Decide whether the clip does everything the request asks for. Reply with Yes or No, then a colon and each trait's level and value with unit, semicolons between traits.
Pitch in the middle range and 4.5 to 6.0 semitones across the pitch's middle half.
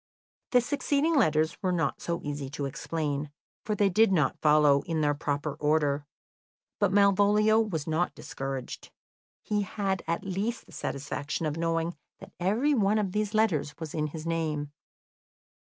Yes: medium, 165 Hz; wide, 5.5 semitones